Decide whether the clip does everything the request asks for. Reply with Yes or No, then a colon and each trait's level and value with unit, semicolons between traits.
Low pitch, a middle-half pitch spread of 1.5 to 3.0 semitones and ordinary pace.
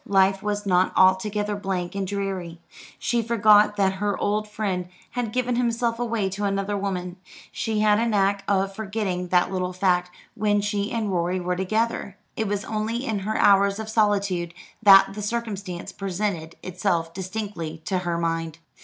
No: high, 200 Hz; narrow, 2.5 semitones; average, 165 wpm